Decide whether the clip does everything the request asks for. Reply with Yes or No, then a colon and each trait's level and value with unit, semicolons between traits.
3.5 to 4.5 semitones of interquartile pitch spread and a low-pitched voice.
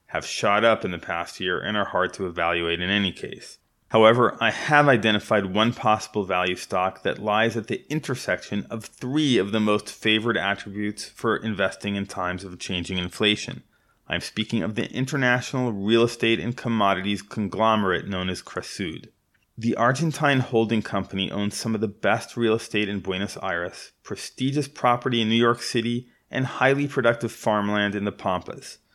No: average, 3.1 semitones; low, 110 Hz